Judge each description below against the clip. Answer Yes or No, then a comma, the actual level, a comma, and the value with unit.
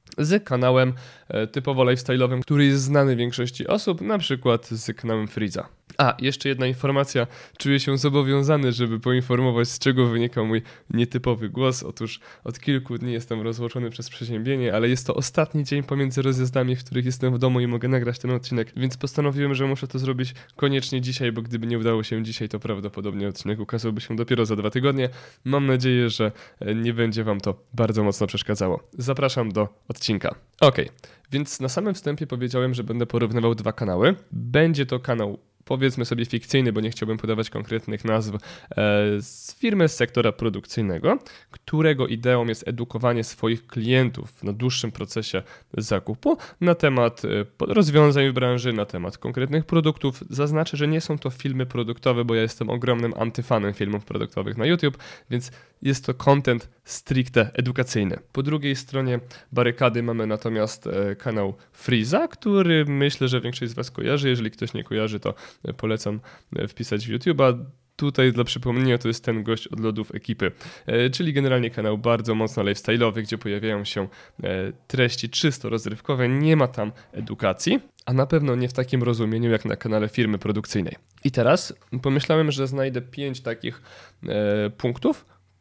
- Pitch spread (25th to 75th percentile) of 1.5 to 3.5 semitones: Yes, average, 3.1 semitones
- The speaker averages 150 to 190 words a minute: Yes, fast, 160 wpm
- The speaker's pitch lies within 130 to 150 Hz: No, low, 120 Hz